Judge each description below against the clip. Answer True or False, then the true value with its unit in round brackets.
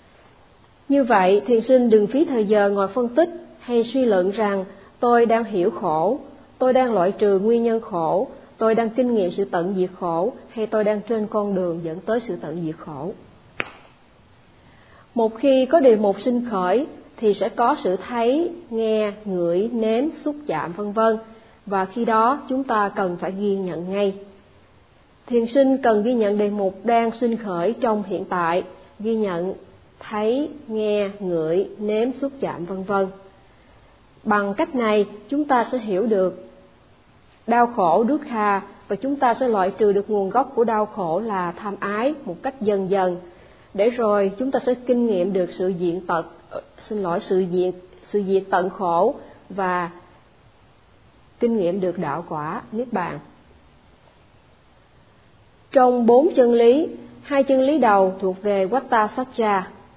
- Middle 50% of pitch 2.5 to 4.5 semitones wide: True (4.2 semitones)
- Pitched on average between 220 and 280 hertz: False (210 Hz)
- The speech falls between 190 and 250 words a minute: False (170 wpm)